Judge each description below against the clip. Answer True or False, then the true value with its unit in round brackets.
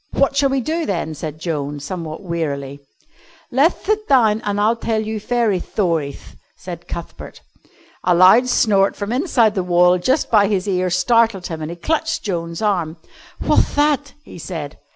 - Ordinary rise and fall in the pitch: False (6.0 semitones)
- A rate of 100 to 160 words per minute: False (170 wpm)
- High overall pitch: True (200 Hz)